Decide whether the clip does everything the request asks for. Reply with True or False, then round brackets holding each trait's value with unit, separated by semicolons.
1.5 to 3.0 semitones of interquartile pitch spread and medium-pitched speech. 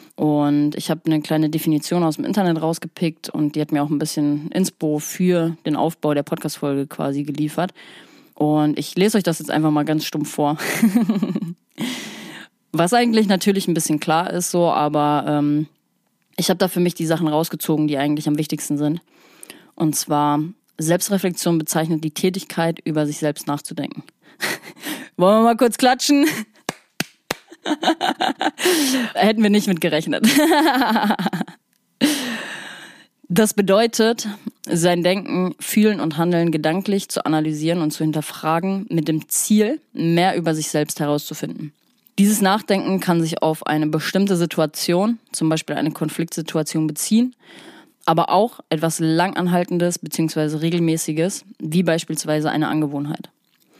False (4.9 semitones; 170 Hz)